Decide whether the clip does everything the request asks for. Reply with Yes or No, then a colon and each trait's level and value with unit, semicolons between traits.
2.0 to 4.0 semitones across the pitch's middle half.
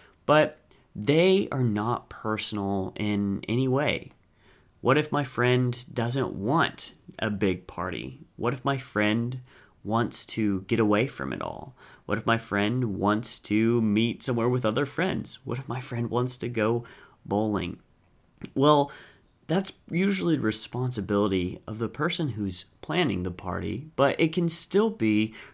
No: average, 4.4 semitones